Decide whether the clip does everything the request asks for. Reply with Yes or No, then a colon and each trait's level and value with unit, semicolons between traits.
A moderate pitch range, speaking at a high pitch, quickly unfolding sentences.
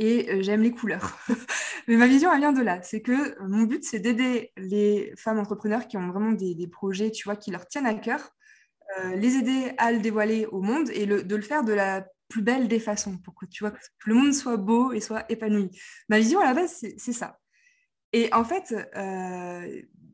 Yes: average, 3.1 semitones; high, 220 Hz; fast, 225 wpm